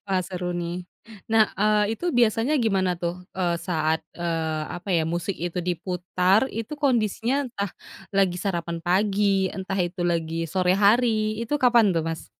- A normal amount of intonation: Yes, average, 3.8 semitones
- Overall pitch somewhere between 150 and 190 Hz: Yes, medium, 185 Hz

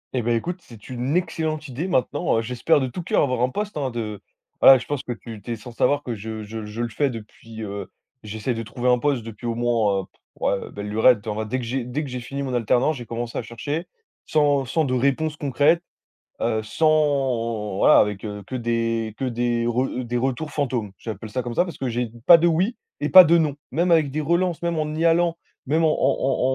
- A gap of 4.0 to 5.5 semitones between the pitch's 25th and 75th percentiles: Yes, average, 4.8 semitones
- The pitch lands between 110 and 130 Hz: Yes, low, 125 Hz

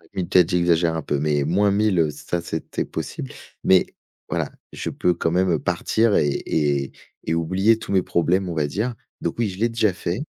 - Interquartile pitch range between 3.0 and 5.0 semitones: Yes, average, 3.6 semitones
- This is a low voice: Yes, very low, 90 Hz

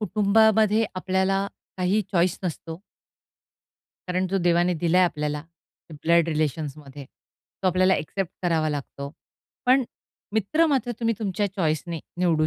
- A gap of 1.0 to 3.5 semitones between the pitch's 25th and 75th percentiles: No, average, 4.1 semitones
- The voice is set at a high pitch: No, medium, 180 Hz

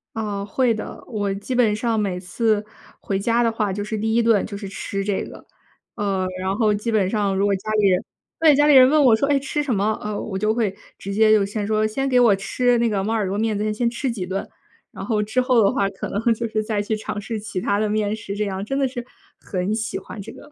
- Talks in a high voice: Yes, high, 215 Hz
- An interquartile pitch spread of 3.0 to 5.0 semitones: No, narrow, 2.5 semitones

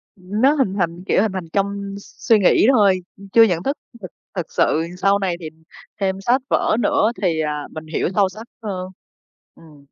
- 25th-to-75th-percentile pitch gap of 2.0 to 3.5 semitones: Yes, average, 3.2 semitones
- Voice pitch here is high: Yes, high, 195 Hz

